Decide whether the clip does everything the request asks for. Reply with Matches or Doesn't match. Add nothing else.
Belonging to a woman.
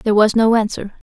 Matches